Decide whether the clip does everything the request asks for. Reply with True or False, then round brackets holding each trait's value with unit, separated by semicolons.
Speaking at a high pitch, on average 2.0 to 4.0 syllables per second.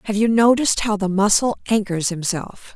False (205 Hz; 5.4 syllables/s)